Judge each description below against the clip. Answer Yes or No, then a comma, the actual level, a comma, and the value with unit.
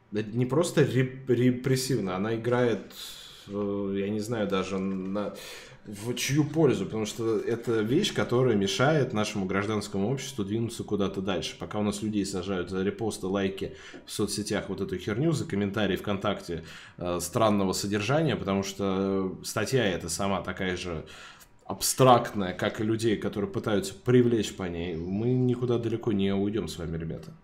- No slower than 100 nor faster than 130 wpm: No, average, 145 wpm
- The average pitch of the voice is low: Yes, low, 105 Hz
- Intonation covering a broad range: No, average, 3.7 semitones